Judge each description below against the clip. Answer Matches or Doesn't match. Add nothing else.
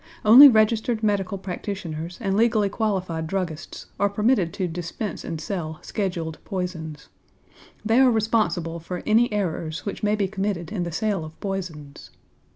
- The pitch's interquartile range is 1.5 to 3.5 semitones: Doesn't match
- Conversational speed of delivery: Matches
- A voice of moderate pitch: Doesn't match